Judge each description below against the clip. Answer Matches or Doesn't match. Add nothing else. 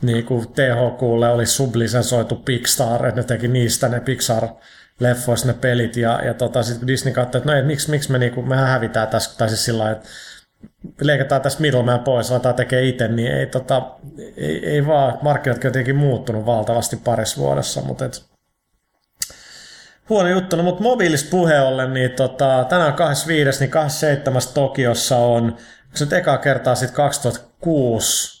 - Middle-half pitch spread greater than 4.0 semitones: Doesn't match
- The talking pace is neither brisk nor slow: Doesn't match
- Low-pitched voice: Matches